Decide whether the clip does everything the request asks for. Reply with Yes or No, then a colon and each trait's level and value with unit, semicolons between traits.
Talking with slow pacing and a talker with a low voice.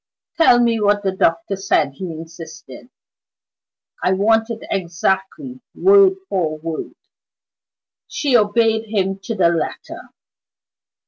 No: slow, 115 wpm; high, 195 Hz